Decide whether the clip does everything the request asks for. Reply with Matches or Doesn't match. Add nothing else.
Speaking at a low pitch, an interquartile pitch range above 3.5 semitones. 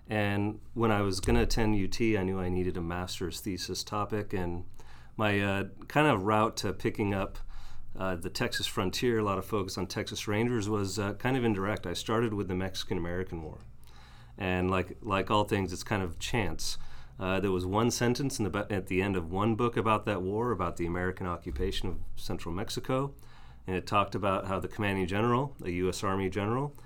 Doesn't match